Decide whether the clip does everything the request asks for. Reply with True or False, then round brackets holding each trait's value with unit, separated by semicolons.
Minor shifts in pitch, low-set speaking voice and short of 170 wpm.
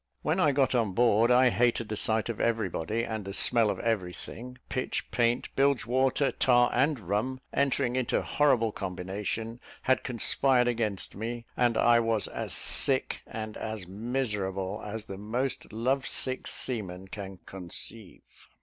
False (3.4 semitones; 115 Hz; 160 wpm)